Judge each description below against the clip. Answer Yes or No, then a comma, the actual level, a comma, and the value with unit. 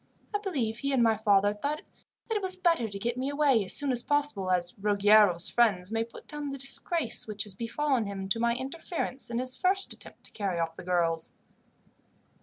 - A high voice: Yes, high, 235 Hz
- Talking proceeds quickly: Yes, fast, 210 wpm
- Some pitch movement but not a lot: No, wide, 6.0 semitones